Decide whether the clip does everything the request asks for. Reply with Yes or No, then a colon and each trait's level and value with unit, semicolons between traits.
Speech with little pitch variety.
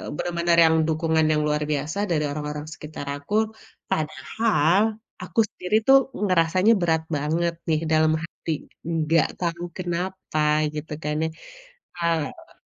Yes: narrow, 2.2 semitones